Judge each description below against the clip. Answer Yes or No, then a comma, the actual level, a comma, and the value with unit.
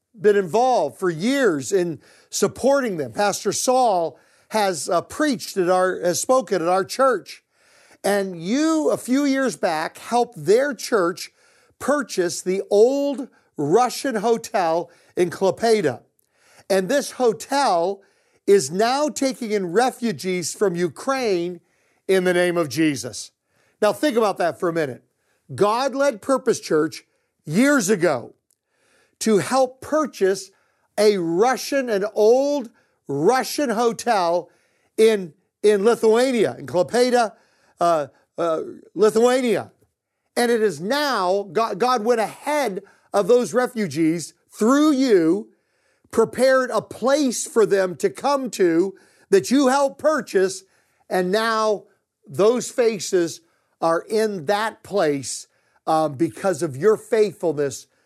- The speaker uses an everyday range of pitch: No, wide, 5.7 semitones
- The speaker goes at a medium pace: No, slow, 120 wpm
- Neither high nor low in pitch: No, high, 215 Hz